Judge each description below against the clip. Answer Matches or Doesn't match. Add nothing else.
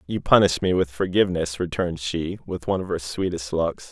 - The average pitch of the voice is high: Doesn't match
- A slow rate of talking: Doesn't match